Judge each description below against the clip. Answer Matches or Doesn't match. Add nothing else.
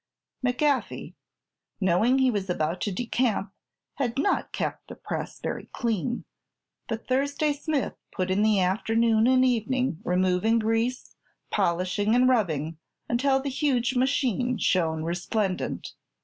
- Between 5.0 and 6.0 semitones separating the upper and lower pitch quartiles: Matches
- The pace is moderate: Doesn't match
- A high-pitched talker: Matches